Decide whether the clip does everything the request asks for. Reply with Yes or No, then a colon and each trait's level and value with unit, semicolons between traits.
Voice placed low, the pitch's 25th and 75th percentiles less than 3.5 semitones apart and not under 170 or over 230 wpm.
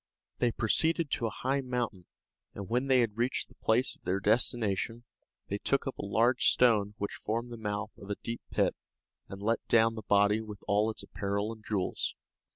Yes: low, 110 Hz; average, 2.9 semitones; average, 195 wpm